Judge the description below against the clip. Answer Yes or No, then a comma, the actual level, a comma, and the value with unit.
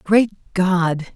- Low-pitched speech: No, medium, 185 Hz